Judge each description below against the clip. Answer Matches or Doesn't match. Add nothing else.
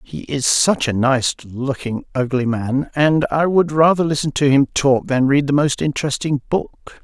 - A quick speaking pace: Doesn't match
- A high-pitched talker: Doesn't match